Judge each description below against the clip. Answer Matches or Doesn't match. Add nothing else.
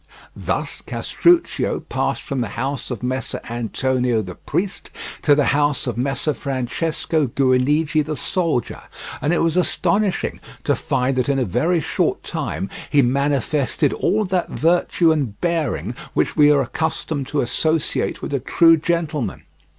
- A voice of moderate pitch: Matches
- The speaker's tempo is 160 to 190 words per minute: Doesn't match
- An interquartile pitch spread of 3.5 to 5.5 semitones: Matches